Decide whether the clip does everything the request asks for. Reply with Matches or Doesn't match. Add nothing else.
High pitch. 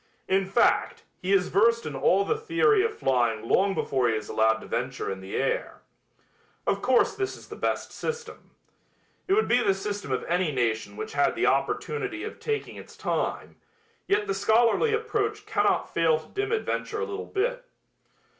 Matches